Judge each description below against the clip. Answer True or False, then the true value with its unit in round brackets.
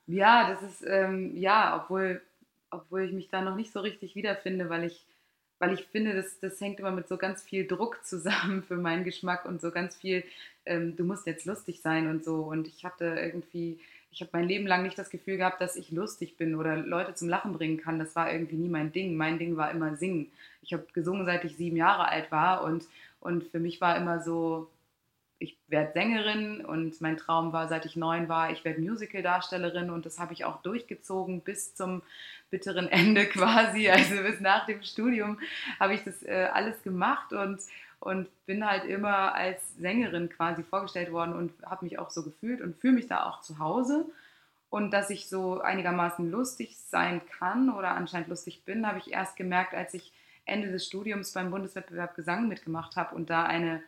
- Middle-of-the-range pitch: True (180 Hz)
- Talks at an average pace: False (205 wpm)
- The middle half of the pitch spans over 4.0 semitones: False (2.4 semitones)